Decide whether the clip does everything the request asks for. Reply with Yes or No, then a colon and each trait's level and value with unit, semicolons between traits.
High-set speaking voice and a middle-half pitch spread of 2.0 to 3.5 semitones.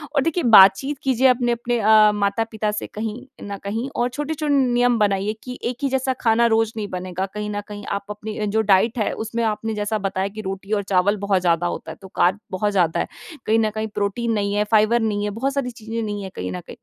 Yes: high, 215 Hz; average, 2.9 semitones